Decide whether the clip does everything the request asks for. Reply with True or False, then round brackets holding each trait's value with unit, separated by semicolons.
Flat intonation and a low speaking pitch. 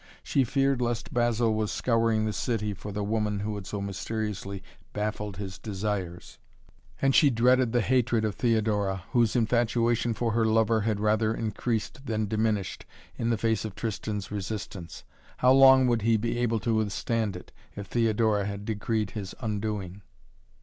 True (2.2 semitones; 110 Hz)